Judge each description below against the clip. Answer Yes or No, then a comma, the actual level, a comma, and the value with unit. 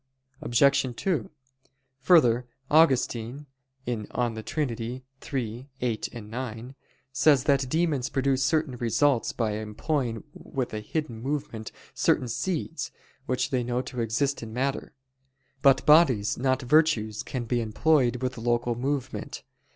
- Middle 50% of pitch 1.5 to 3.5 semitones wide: Yes, average, 3.2 semitones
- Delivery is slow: Yes, slow, 120 wpm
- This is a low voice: Yes, low, 125 Hz